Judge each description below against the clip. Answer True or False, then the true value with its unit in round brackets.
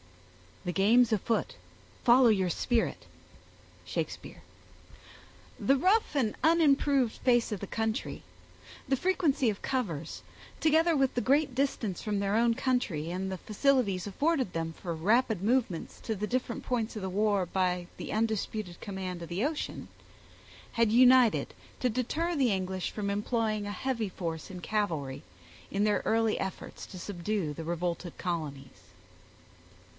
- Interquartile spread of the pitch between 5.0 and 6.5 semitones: True (5.4 semitones)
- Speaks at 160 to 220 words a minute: False (145 wpm)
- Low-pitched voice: False (215 Hz)